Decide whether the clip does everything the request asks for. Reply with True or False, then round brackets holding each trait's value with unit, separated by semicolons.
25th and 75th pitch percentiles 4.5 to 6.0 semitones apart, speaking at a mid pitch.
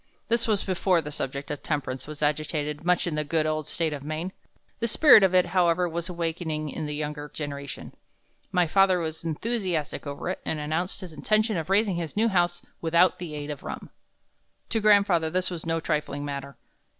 False (3.5 semitones; 165 Hz)